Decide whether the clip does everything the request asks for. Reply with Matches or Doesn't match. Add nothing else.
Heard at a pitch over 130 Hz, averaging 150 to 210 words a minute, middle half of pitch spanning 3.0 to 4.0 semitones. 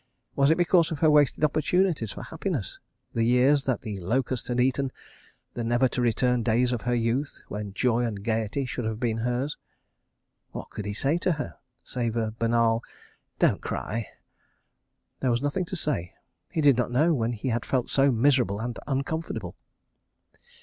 Doesn't match